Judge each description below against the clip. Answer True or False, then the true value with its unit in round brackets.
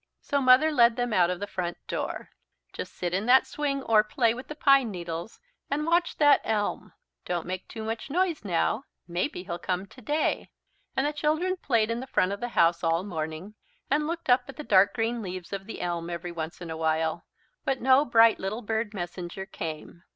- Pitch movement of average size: False (7.1 semitones)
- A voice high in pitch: True (215 Hz)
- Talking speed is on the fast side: True (210 wpm)